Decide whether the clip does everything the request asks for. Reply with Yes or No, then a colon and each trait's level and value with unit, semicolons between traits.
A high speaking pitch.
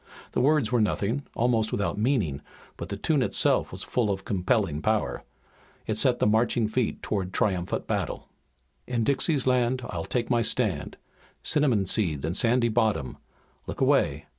No: low, 110 Hz